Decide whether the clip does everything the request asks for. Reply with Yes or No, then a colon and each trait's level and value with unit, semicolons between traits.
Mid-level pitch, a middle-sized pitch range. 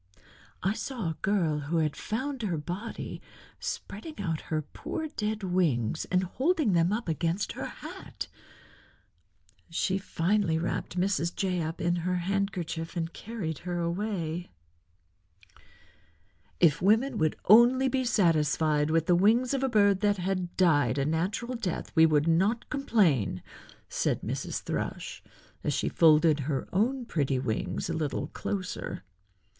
Yes: medium, 180 Hz; average, 4.6 semitones